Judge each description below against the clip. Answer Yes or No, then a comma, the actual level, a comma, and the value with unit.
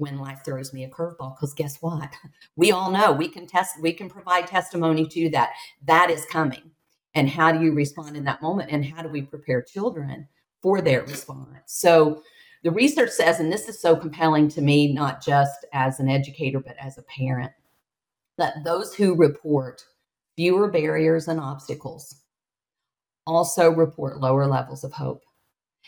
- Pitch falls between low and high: Yes, medium, 155 Hz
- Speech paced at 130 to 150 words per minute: No, average, 175 wpm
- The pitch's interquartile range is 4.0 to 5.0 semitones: No, average, 3.2 semitones